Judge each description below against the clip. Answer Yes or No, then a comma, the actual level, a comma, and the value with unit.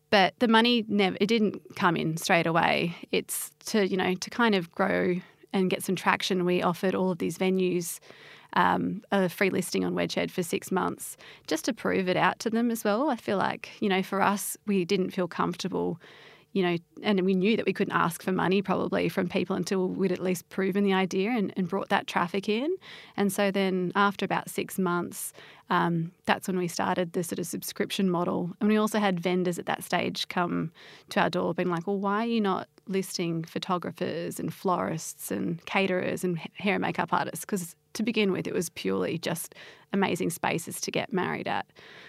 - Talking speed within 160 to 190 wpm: No, fast, 205 wpm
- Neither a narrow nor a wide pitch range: No, narrow, 2.1 semitones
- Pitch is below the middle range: No, high, 190 Hz